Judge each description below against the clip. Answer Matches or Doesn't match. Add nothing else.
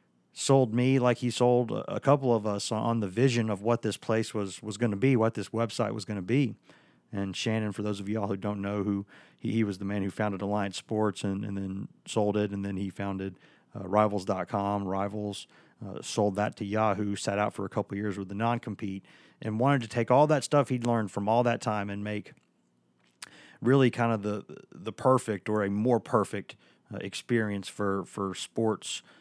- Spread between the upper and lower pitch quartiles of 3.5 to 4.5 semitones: Doesn't match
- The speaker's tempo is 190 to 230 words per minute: Matches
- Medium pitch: Doesn't match